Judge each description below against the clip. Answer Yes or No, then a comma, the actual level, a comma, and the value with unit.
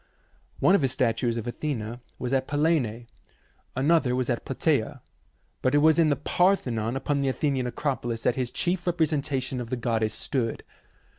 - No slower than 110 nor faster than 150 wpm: No, average, 165 wpm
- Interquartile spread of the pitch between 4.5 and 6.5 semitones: No, average, 3.8 semitones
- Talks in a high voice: No, low, 130 Hz